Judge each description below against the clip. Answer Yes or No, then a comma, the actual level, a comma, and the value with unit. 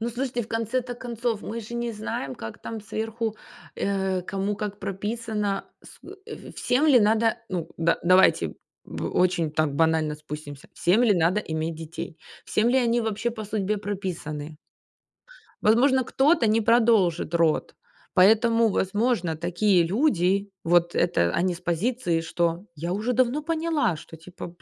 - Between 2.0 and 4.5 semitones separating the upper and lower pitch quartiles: No, average, 5.3 semitones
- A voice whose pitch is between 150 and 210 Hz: Yes, high, 205 Hz